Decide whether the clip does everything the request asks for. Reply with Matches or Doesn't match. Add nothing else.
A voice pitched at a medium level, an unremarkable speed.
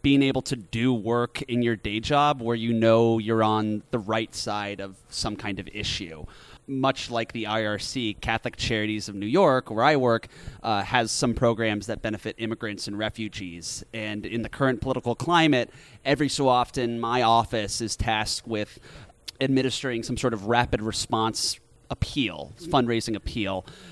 Doesn't match